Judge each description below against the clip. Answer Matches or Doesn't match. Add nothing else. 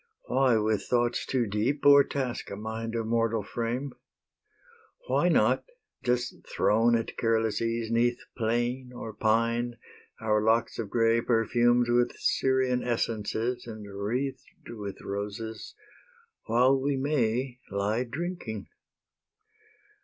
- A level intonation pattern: Matches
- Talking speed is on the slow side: Matches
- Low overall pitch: Matches